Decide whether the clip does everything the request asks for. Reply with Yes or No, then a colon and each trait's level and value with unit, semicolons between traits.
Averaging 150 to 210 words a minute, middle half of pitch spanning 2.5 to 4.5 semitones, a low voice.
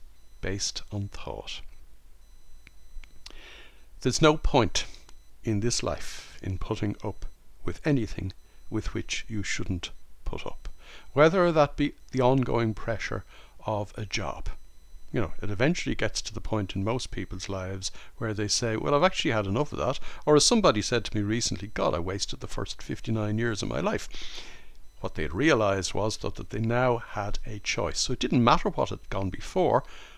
Yes: average, 175 wpm; average, 3.8 semitones; low, 105 Hz